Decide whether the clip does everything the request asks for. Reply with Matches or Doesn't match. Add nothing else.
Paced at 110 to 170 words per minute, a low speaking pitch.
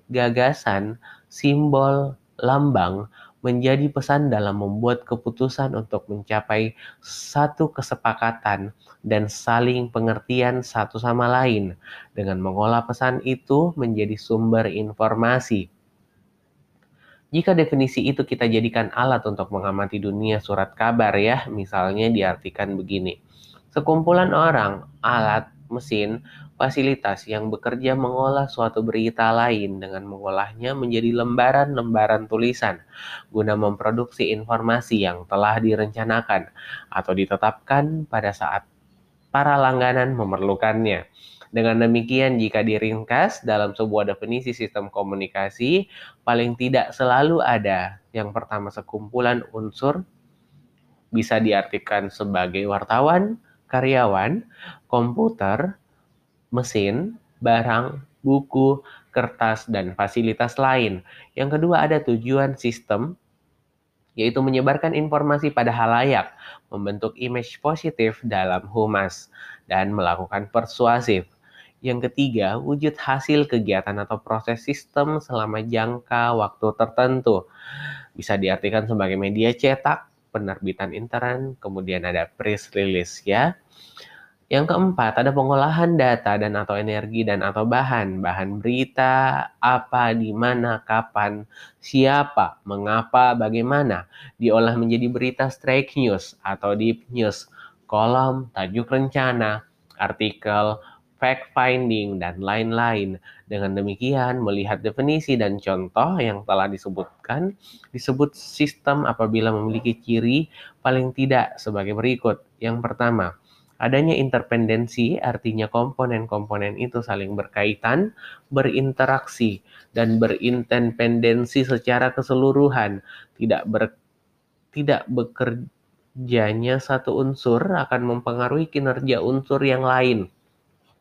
Doesn't match